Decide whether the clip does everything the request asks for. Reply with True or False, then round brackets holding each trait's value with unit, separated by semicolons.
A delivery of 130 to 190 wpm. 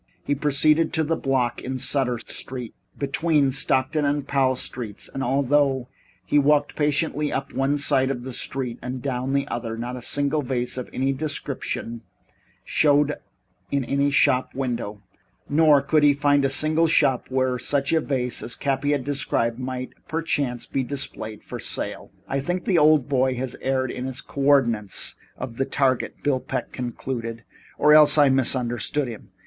True (170 wpm)